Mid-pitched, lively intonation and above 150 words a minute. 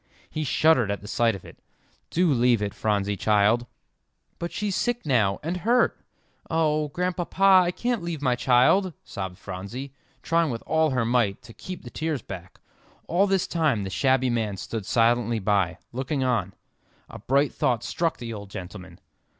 No: low, 125 Hz; wide, 7.6 semitones; average, 170 wpm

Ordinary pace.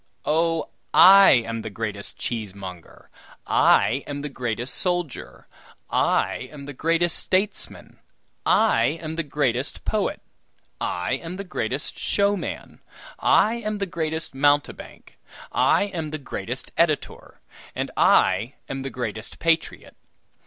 No: slow, 125 wpm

